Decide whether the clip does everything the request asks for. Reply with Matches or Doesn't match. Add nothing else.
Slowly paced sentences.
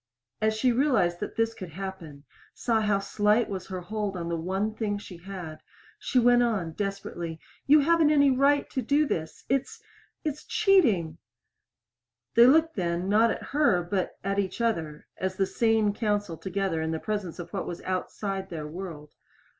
Doesn't match